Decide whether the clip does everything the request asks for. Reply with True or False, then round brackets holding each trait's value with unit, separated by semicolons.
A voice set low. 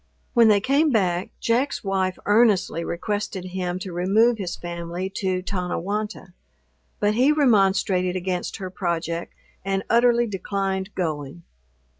False (190 Hz)